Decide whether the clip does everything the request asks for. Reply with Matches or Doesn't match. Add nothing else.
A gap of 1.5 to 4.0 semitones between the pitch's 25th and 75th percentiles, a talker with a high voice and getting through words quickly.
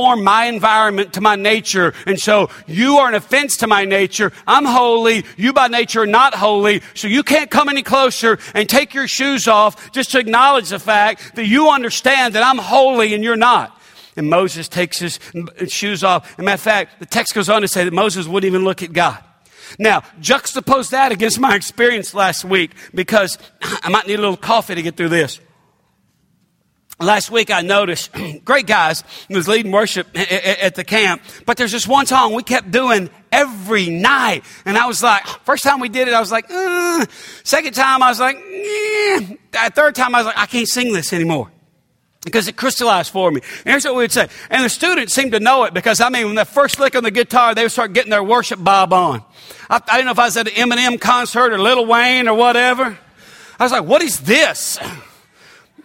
Doesn't match